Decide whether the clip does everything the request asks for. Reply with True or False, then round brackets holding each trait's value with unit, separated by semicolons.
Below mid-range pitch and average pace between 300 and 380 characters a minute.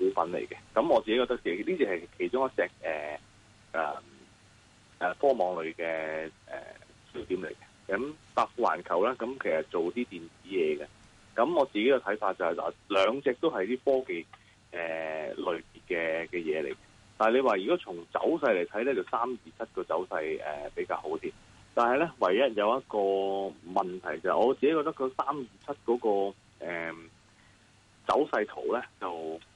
False (105 Hz; 250 characters per minute)